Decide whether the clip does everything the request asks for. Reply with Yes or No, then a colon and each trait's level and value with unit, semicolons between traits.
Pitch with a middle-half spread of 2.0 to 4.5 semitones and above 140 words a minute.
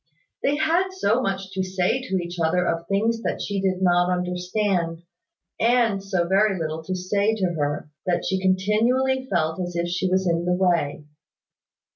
Yes: average, 3.2 semitones; average, 175 wpm